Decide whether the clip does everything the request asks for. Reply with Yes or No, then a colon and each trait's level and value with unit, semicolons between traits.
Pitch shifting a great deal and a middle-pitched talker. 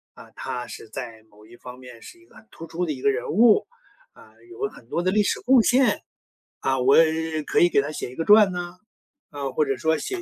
Yes: wide, 8.6 semitones; medium, 155 Hz